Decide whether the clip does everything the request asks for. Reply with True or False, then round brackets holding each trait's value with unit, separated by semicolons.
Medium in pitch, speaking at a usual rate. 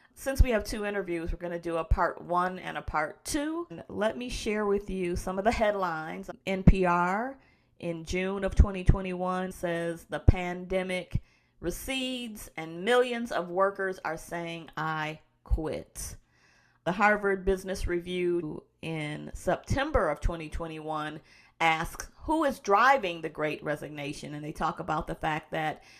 True (180 Hz; 150 wpm)